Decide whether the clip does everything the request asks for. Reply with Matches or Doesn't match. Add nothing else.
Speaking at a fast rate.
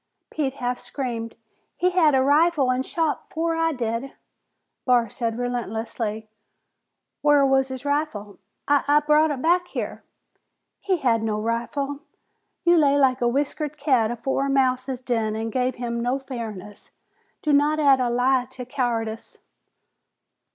Doesn't match